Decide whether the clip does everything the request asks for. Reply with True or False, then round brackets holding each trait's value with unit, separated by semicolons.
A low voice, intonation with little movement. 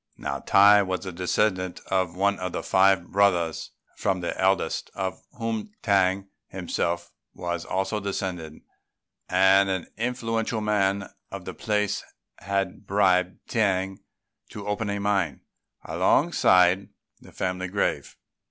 True (95 Hz; 1.8 semitones)